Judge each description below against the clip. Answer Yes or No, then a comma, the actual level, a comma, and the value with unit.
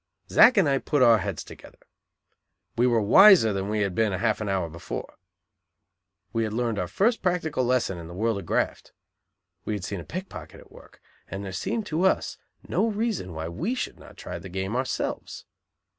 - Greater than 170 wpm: Yes, average, 195 wpm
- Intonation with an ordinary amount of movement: No, wide, 8.6 semitones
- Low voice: Yes, low, 110 Hz